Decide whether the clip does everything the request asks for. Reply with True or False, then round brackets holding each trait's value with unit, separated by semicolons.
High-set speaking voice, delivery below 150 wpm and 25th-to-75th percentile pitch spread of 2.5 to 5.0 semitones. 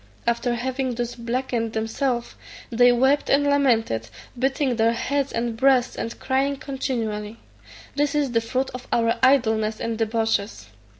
True (240 Hz; 140 wpm; 2.8 semitones)